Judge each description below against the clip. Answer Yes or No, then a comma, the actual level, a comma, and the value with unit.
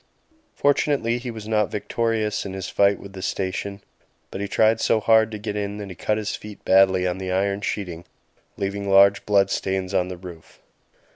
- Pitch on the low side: Yes, low, 100 Hz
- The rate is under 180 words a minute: No, average, 195 wpm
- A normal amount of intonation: No, narrow, 2.0 semitones